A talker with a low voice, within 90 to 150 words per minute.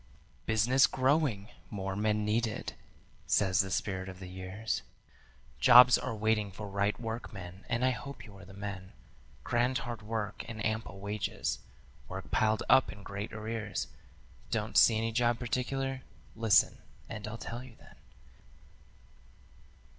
Yes: low, 110 Hz; average, 140 wpm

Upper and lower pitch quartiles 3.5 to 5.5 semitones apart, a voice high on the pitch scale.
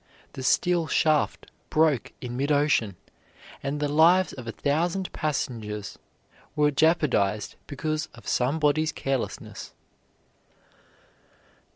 No: average, 3.8 semitones; medium, 145 Hz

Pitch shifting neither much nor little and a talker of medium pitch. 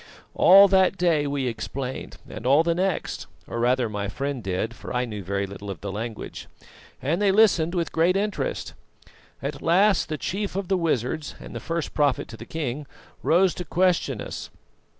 No: wide, 7.3 semitones; medium, 150 Hz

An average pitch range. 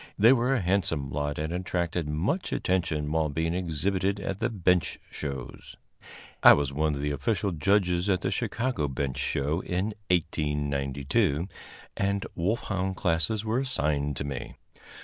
Yes: average, 5.0 semitones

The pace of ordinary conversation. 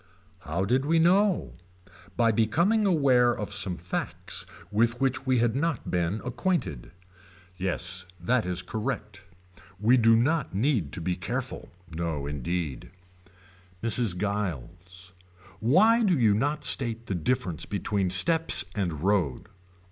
No: slow, 130 wpm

